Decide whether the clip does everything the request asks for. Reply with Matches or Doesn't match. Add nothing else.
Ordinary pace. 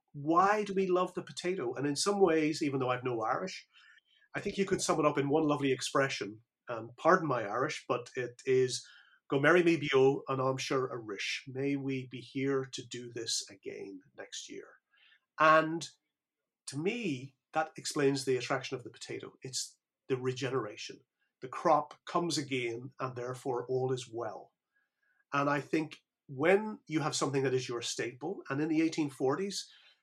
Matches